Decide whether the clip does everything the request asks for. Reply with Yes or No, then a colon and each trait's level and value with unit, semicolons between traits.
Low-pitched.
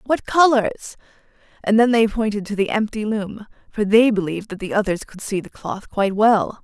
No: high, 215 Hz